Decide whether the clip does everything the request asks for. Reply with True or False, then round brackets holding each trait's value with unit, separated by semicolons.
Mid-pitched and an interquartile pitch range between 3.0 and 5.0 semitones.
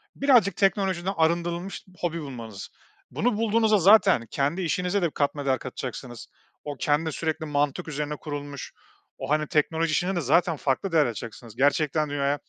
True (155 Hz; 4.0 semitones)